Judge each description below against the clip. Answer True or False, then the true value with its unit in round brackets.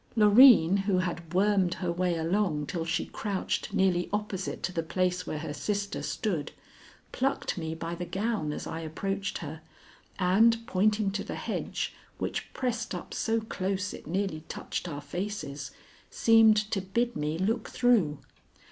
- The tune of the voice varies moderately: True (4.2 semitones)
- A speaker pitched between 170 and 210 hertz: True (190 Hz)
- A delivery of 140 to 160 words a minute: True (155 wpm)